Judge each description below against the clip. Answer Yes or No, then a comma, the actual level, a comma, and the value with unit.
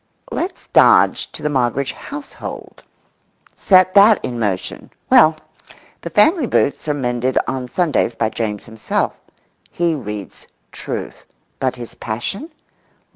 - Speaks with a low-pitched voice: Yes, low, 130 Hz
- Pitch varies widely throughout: Yes, wide, 7.6 semitones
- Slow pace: Yes, slow, 125 wpm